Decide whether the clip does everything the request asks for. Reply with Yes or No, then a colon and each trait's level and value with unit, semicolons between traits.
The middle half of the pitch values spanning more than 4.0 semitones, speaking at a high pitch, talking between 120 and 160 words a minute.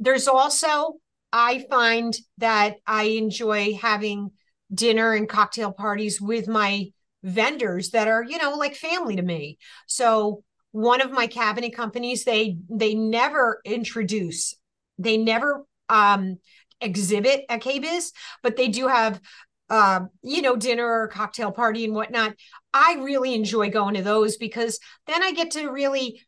No: average, 3.1 semitones; high, 225 Hz; average, 150 wpm